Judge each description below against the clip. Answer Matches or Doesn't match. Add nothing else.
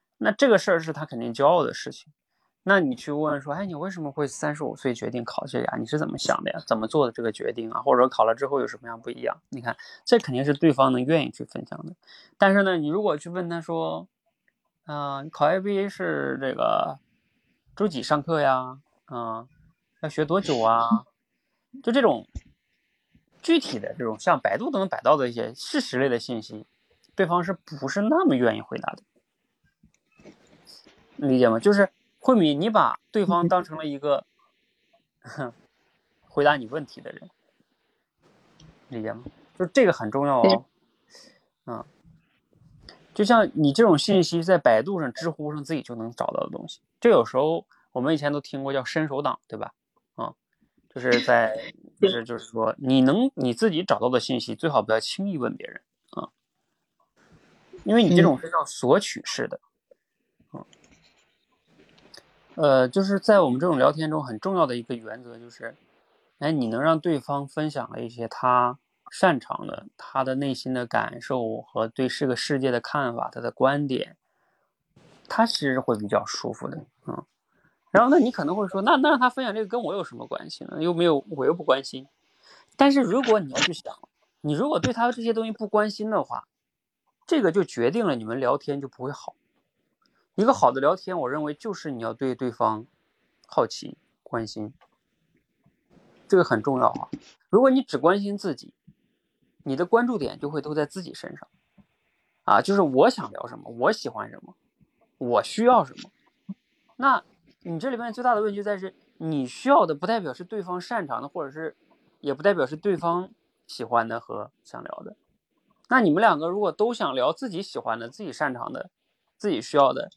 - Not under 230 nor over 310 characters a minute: Matches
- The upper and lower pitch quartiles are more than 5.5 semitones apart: Matches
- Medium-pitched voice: Matches